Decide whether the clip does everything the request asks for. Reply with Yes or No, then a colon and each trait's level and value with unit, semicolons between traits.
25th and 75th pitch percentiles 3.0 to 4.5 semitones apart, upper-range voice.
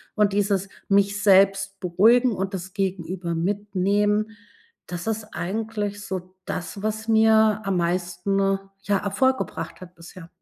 No: narrow, 2.4 semitones; high, 195 Hz